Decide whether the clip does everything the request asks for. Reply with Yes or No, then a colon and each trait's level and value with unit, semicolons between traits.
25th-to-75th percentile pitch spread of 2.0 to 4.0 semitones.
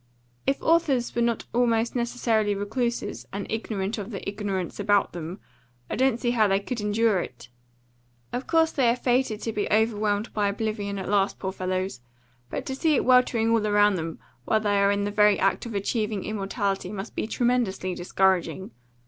Yes: average, 3.0 semitones